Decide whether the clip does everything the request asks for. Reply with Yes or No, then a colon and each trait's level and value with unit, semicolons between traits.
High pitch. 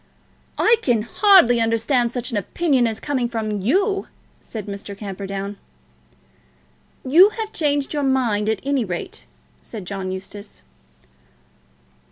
Yes: high, 235 Hz